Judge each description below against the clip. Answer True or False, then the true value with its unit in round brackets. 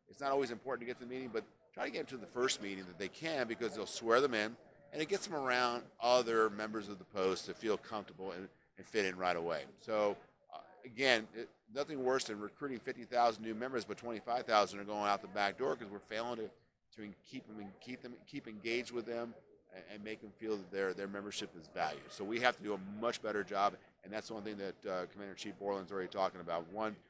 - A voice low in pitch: True (110 Hz)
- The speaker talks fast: True (250 wpm)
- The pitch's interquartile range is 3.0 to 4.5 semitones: True (3.3 semitones)